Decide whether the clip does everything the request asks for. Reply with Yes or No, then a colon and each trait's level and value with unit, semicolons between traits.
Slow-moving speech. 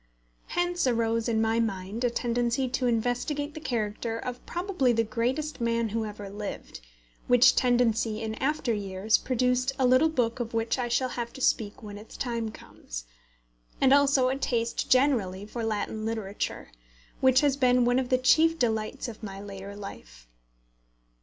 No: average, 165 wpm